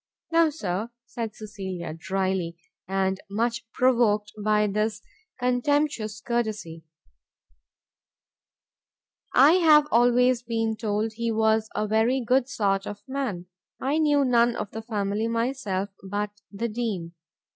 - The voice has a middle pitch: No, high, 220 Hz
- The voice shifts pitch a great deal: No, average, 3.2 semitones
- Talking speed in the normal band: No, slow, 120 wpm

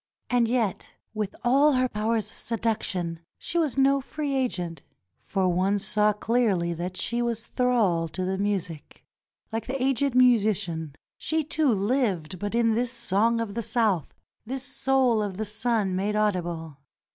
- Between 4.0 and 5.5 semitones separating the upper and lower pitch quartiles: Yes, average, 4.8 semitones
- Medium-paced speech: Yes, average, 160 wpm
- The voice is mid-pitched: No, high, 220 Hz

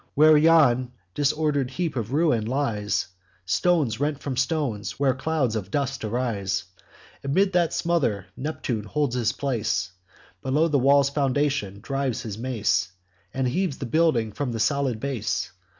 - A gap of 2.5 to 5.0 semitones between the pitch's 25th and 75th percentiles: Yes, average, 4.5 semitones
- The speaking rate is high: No, average, 145 wpm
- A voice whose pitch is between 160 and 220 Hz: No, low, 130 Hz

